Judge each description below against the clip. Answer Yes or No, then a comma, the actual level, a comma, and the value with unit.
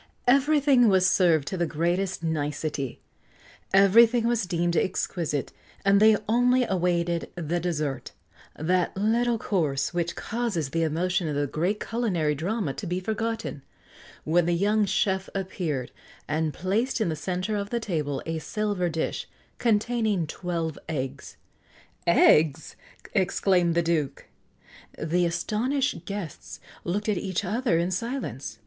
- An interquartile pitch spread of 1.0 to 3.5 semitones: No, average, 4.7 semitones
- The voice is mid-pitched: Yes, medium, 180 Hz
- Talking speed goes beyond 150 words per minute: No, slow, 135 wpm